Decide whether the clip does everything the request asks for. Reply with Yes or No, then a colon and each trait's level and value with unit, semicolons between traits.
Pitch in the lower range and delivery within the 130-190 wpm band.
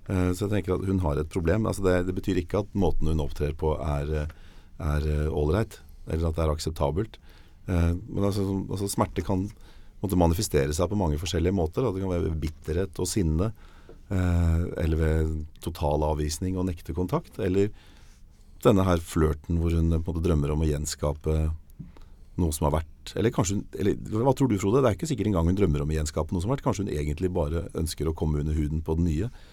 No: very low, 85 Hz; fast, 205 wpm